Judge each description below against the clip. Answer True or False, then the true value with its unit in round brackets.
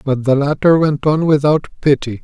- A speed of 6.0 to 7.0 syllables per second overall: False (5.0 syllables/s)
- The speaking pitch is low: False (145 Hz)